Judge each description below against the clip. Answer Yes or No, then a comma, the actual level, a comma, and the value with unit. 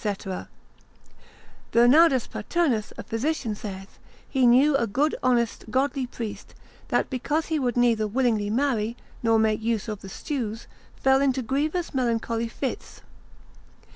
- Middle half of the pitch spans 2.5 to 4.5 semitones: Yes, average, 3.6 semitones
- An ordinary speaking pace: No, slow, 130 wpm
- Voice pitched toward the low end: No, high, 245 Hz